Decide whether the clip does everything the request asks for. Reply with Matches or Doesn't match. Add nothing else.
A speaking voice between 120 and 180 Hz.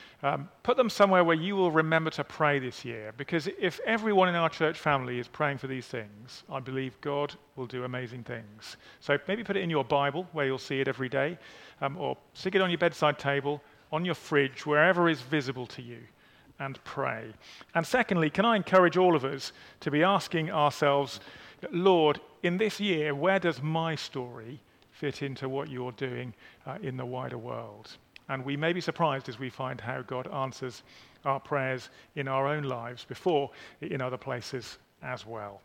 Matches